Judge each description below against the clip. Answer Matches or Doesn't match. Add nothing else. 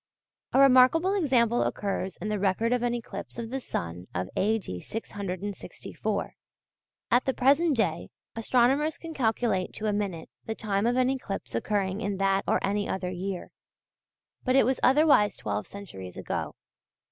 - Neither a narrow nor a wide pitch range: Matches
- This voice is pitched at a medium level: Doesn't match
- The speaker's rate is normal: Matches